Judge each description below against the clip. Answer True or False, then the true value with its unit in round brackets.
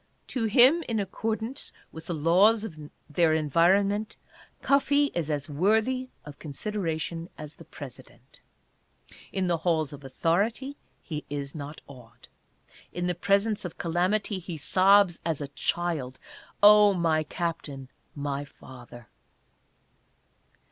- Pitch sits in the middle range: True (170 Hz)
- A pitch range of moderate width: False (5.7 semitones)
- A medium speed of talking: False (130 wpm)